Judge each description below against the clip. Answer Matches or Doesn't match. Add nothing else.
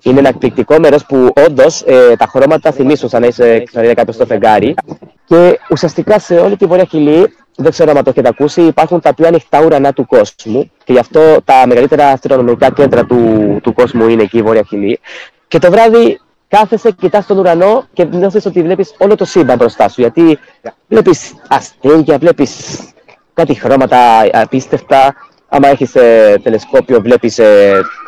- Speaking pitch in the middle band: Matches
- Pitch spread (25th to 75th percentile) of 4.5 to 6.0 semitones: Doesn't match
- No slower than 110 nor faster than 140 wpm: Doesn't match